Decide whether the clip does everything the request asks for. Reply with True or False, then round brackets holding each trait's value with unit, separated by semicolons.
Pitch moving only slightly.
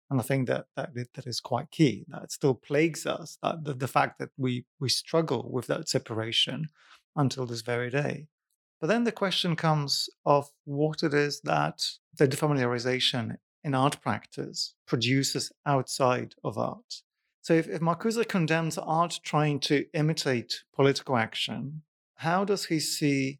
False (3.6 semitones)